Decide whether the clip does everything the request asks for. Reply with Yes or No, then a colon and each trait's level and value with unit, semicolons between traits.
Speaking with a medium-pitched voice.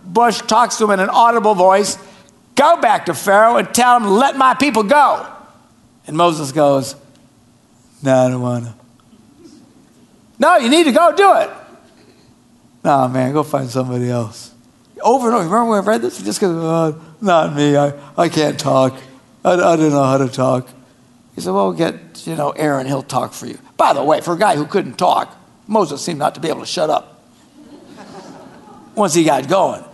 Yes: medium, 175 Hz